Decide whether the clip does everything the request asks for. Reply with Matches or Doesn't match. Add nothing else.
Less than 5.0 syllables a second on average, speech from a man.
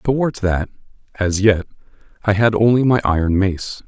Matches